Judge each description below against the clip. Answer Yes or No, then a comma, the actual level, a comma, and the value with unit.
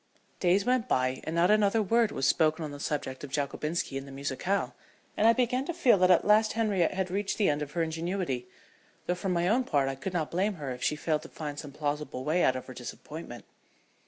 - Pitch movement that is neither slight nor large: No, wide, 5.7 semitones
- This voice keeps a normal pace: No, fast, 235 wpm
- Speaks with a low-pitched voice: No, medium, 165 Hz